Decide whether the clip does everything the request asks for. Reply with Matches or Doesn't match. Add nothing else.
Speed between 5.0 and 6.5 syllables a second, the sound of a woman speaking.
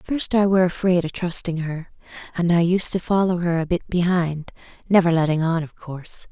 Matches